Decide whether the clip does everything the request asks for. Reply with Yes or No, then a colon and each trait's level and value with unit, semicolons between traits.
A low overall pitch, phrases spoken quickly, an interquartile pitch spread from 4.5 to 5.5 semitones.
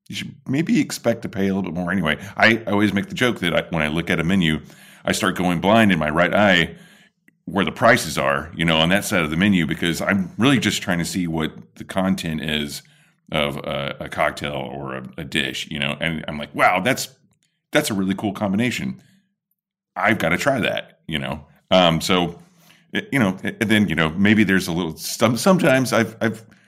Yes: very low, 90 Hz; fast, 225 wpm; average, 5.1 semitones